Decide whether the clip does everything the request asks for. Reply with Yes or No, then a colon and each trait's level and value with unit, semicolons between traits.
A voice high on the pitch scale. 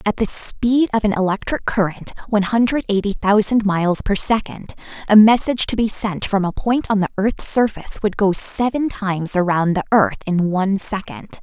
Yes: high, 205 Hz